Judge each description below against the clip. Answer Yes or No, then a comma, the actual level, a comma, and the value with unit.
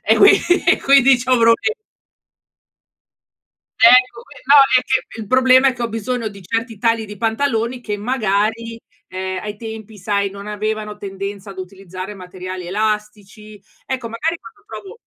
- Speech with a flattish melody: No, average, 3.6 semitones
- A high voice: Yes, high, 220 Hz